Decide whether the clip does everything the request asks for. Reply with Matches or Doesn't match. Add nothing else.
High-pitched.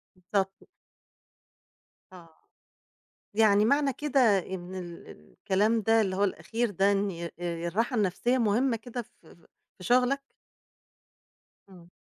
Matches